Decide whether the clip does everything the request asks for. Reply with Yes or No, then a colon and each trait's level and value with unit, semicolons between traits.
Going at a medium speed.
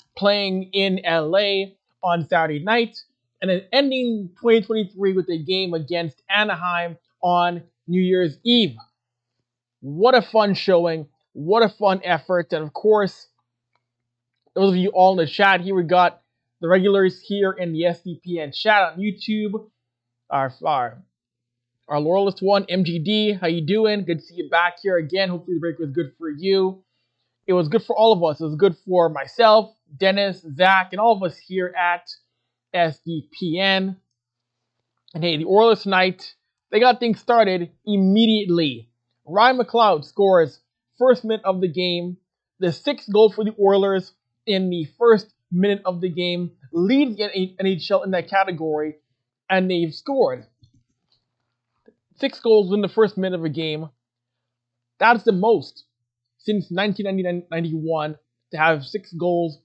Yes: average, 155 wpm